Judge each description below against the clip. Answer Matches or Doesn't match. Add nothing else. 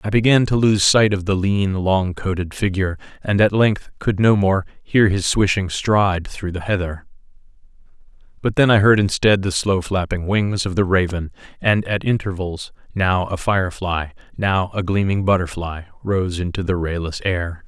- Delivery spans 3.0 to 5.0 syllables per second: Matches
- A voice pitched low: Matches